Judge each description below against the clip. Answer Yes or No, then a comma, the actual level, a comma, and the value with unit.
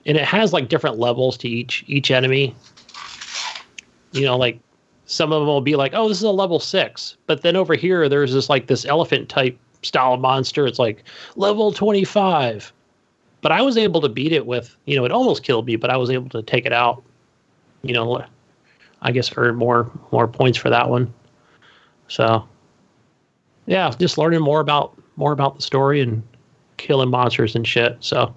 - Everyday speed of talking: Yes, average, 190 wpm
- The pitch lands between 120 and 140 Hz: Yes, low, 135 Hz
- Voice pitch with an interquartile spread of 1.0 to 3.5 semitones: No, average, 4.2 semitones